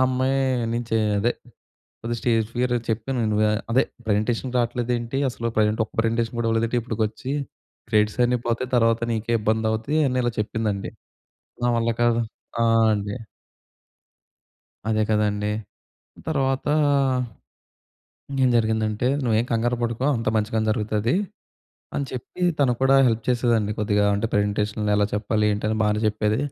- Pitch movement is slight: Yes, narrow, 2.2 semitones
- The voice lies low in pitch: Yes, low, 115 Hz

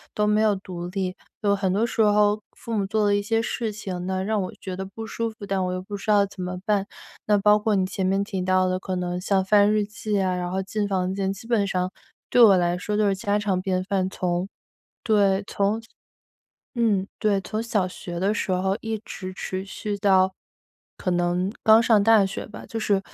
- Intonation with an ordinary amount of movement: No, narrow, 2.1 semitones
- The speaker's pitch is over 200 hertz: No, high, 195 Hz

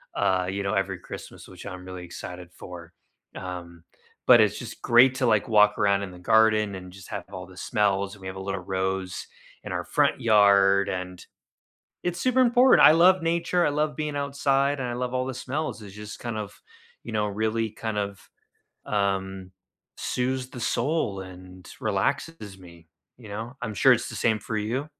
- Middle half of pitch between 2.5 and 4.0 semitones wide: No, average, 4.9 semitones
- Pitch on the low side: Yes, low, 105 Hz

